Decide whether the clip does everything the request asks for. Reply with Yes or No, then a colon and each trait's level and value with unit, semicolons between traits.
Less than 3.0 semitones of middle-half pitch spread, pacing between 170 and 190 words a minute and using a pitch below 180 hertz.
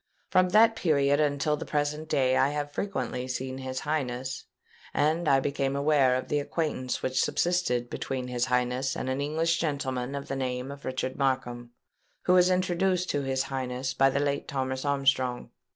Yes: narrow, 2.5 semitones; average, 175 wpm; low, 135 Hz